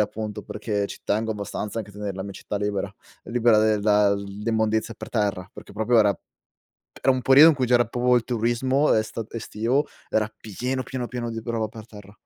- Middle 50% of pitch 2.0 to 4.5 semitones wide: Yes, narrow, 2.6 semitones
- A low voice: Yes, low, 110 Hz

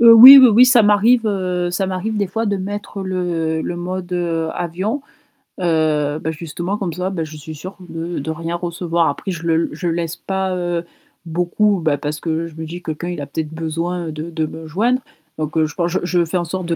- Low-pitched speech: No, medium, 175 Hz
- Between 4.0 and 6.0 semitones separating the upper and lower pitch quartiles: No, average, 2.8 semitones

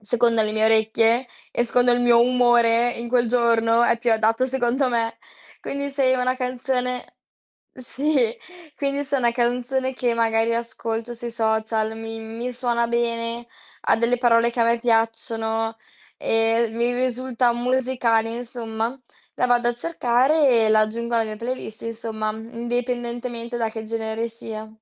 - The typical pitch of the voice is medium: No, high, 235 Hz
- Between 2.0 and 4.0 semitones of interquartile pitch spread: No, narrow, 1.6 semitones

